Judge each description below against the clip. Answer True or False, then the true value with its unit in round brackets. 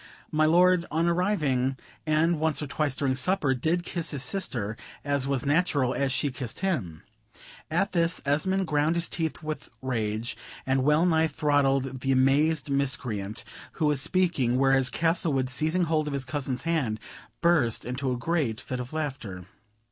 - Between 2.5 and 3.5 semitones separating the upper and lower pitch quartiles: False (3.9 semitones)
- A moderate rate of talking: True (160 wpm)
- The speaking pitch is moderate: True (145 Hz)